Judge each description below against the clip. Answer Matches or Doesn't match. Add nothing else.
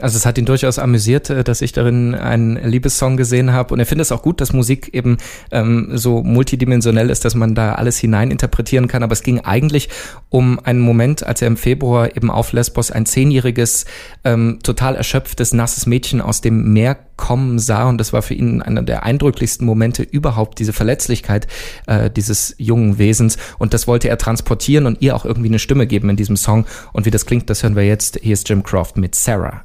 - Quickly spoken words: Matches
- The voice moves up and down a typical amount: Doesn't match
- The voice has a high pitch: Doesn't match